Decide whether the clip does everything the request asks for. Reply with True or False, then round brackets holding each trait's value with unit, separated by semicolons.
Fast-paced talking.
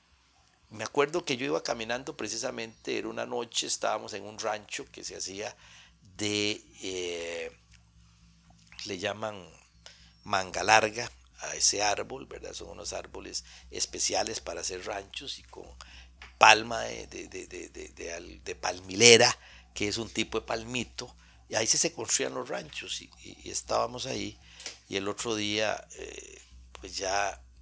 False (150 wpm)